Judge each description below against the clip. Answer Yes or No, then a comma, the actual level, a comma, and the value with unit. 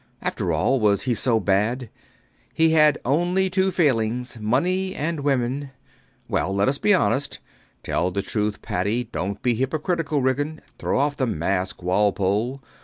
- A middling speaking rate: Yes, average, 150 wpm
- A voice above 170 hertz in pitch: No, low, 125 Hz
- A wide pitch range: Yes, wide, 6.3 semitones